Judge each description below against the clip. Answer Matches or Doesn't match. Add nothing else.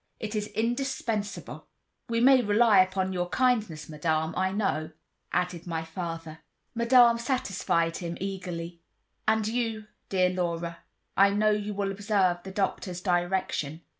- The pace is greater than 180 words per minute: Doesn't match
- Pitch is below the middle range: Doesn't match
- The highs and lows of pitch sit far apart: Doesn't match